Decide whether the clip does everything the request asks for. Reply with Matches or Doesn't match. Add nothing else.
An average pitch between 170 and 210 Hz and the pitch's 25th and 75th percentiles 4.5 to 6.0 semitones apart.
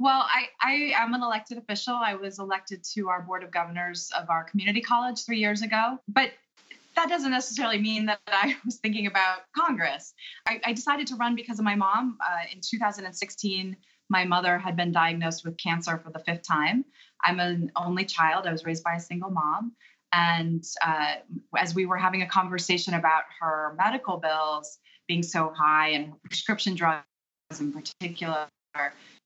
Matches